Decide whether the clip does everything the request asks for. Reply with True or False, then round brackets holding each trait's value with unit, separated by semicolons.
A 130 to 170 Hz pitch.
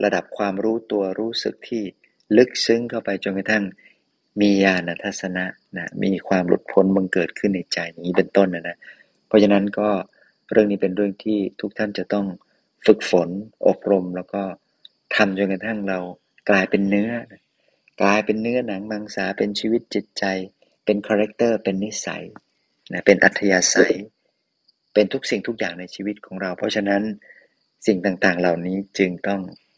False (100 Hz)